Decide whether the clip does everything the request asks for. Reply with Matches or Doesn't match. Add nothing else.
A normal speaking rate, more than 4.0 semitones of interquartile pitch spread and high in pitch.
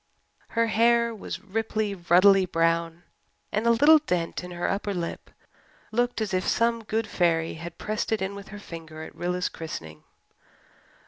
Matches